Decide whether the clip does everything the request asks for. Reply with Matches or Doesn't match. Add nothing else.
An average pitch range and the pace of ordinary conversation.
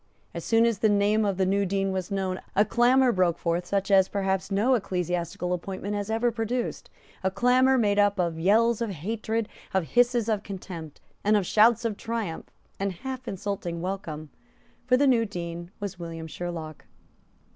Matches